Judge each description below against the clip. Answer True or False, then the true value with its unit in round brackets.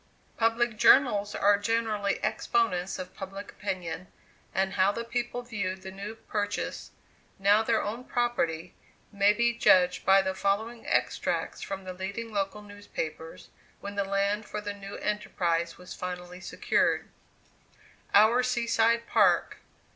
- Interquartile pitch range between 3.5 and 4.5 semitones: False (3.1 semitones)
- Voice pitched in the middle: False (205 Hz)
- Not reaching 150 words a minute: True (140 wpm)